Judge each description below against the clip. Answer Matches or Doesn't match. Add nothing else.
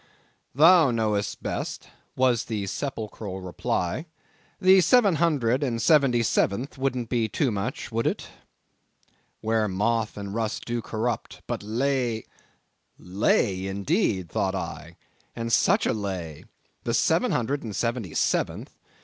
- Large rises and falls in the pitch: Doesn't match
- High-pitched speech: Doesn't match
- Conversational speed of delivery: Doesn't match